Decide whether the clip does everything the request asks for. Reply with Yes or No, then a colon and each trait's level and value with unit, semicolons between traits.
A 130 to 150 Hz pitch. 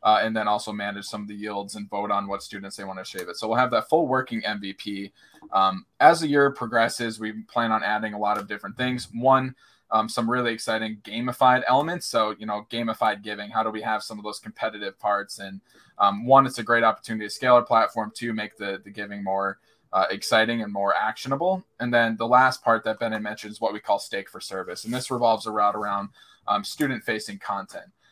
No: low, 110 Hz